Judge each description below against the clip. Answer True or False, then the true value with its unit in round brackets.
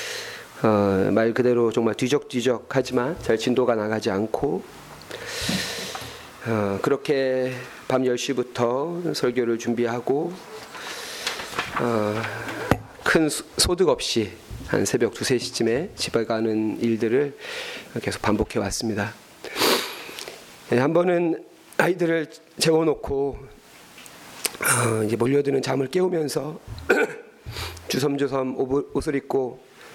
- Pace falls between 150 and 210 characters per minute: True (200 characters per minute)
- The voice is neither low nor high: False (125 Hz)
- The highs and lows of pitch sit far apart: False (4.4 semitones)